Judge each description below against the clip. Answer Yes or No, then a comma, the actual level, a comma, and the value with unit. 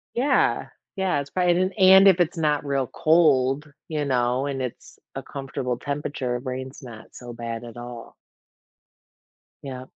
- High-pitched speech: No, low, 135 Hz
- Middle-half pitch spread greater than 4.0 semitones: Yes, average, 4.4 semitones